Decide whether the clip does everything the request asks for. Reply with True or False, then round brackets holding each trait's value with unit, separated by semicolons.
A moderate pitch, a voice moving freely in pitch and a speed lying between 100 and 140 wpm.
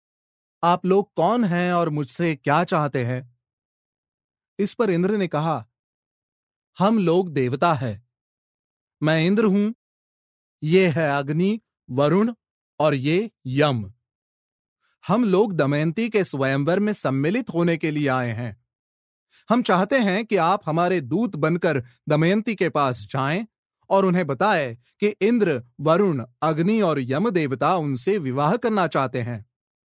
True (160 Hz; 6.5 semitones; 135 wpm)